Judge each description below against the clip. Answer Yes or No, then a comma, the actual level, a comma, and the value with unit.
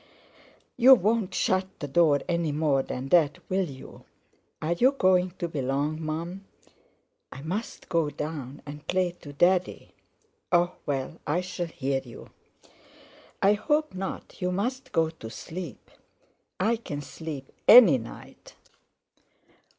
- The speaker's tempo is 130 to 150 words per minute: Yes, slow, 135 wpm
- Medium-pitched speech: Yes, medium, 170 Hz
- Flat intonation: No, average, 4.4 semitones